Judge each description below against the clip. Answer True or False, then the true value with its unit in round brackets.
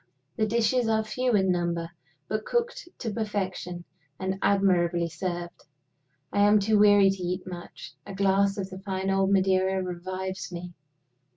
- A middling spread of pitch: False (2.3 semitones)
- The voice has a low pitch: False (190 Hz)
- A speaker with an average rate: True (155 wpm)